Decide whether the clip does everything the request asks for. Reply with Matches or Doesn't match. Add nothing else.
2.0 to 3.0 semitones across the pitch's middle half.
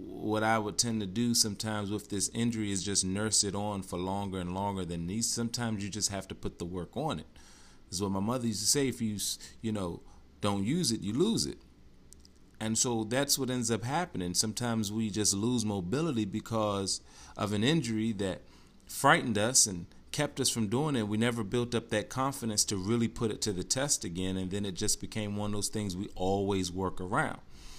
Doesn't match